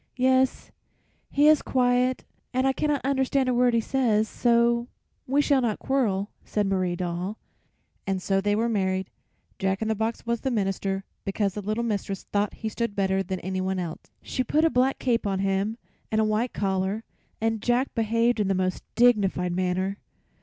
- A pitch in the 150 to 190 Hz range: No, high, 215 Hz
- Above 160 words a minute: Yes, average, 180 wpm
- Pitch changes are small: No, average, 4.3 semitones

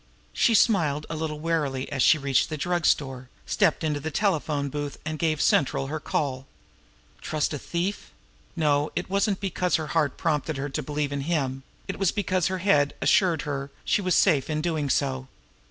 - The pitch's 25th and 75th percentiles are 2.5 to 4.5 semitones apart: Yes, average, 3.3 semitones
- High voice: No, medium, 150 Hz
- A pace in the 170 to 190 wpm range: Yes, average, 185 wpm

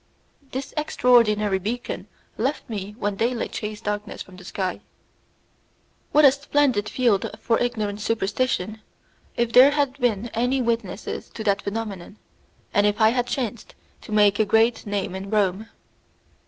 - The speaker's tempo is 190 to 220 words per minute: No, average, 145 wpm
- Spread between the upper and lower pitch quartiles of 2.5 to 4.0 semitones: Yes, average, 3.1 semitones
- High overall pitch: Yes, high, 220 Hz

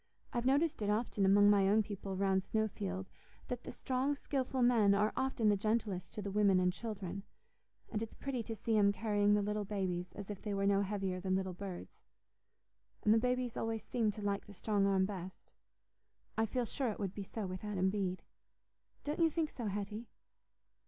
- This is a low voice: No, high, 205 Hz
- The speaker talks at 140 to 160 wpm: No, average, 200 wpm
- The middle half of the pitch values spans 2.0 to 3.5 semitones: Yes, narrow, 2.6 semitones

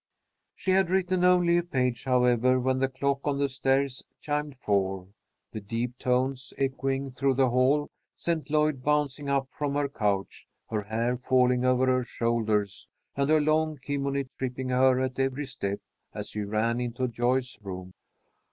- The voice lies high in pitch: No, low, 130 Hz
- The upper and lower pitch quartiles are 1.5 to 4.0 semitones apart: Yes, narrow, 2.5 semitones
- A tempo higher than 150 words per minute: Yes, average, 160 wpm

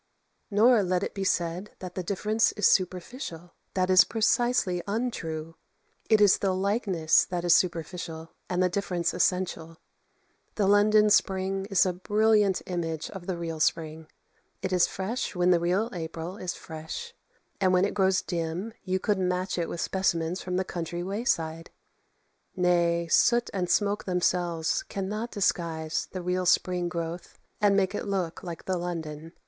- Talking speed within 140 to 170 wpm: Yes, average, 160 wpm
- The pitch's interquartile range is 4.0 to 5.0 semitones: No, average, 2.7 semitones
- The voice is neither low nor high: Yes, medium, 180 Hz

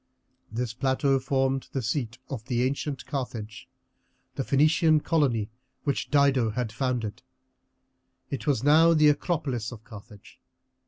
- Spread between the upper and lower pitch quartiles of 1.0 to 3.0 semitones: No, average, 3.5 semitones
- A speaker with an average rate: No, slow, 125 wpm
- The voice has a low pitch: Yes, low, 130 Hz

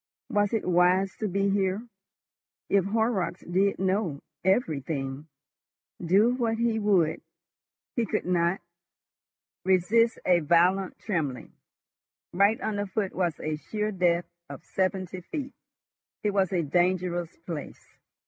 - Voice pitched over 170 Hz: Yes, high, 190 Hz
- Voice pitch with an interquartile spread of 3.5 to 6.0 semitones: No, average, 3.1 semitones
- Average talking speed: No, slow, 120 wpm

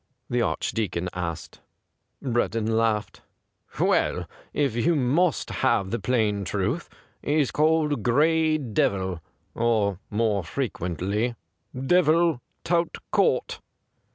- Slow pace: Yes, slow, 110 wpm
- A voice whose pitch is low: Yes, low, 115 Hz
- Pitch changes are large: Yes, wide, 6.7 semitones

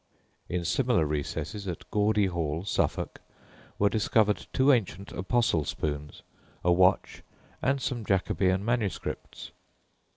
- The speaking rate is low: Yes, slow, 110 wpm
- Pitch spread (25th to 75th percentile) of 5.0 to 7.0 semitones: No, average, 4.3 semitones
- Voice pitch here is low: Yes, very low, 95 Hz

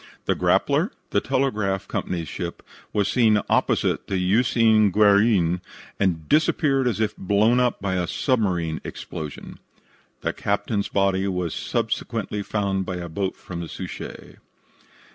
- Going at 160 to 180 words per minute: No, slow, 135 wpm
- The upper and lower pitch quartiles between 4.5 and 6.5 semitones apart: No, average, 3.2 semitones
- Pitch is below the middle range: Yes, low, 100 Hz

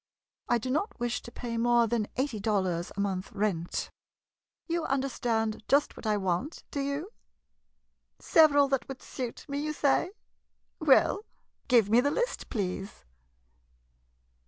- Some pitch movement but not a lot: Yes, average, 5.0 semitones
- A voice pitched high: Yes, high, 240 Hz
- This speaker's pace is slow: No, average, 145 wpm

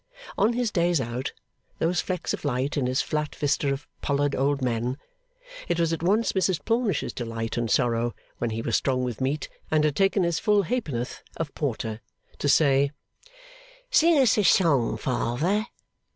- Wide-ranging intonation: Yes, wide, 6.4 semitones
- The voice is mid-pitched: Yes, medium, 145 Hz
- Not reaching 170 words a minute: No, average, 175 wpm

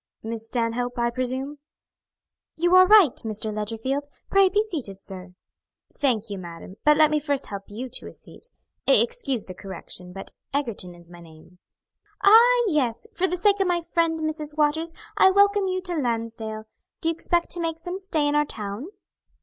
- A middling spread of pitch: No, wide, 8.1 semitones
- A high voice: Yes, very high, 285 Hz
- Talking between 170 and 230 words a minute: Yes, average, 180 wpm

